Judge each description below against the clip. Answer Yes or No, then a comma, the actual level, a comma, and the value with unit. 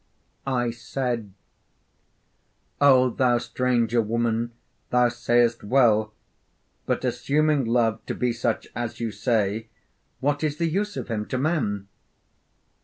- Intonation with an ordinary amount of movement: No, narrow, 2.3 semitones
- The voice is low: Yes, low, 120 Hz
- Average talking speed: No, slow, 120 wpm